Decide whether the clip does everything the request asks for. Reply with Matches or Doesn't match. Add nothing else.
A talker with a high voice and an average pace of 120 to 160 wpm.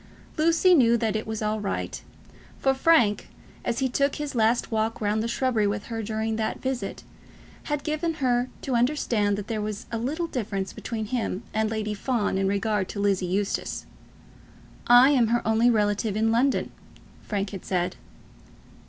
Doesn't match